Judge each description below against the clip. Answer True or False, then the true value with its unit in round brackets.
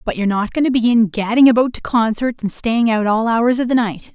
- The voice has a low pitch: False (230 Hz)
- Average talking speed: False (260 wpm)